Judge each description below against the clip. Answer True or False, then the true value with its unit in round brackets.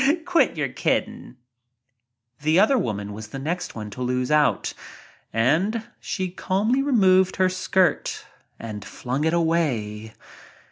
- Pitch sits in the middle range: True (160 Hz)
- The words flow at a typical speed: False (130 wpm)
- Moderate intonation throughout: False (8.6 semitones)